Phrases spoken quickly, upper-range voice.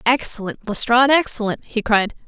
No: slow, 130 wpm; high, 230 Hz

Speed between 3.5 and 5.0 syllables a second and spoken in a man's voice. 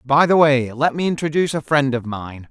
No: 5.4 syllables/s; male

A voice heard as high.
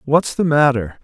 No: medium, 140 Hz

